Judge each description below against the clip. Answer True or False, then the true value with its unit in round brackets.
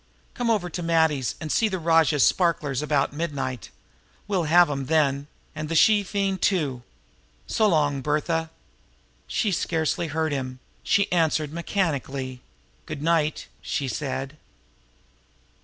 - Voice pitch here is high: False (155 Hz)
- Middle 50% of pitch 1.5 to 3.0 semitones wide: False (3.5 semitones)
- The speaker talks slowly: True (130 wpm)